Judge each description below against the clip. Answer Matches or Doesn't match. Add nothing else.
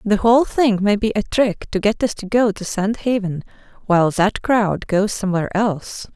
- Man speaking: Doesn't match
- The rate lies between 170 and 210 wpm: Matches